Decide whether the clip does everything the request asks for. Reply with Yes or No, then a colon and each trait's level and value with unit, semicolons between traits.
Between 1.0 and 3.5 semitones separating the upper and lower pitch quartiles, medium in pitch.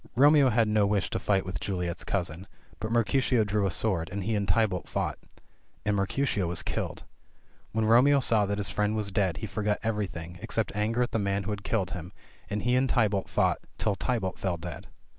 No: average, 2.9 semitones; low, 105 Hz